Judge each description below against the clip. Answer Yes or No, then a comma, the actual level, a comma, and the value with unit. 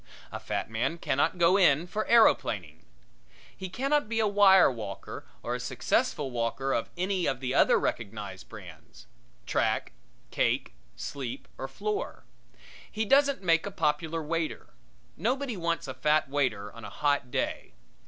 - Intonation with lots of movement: Yes, wide, 8.0 semitones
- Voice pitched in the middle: Yes, medium, 155 Hz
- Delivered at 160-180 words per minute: No, average, 150 wpm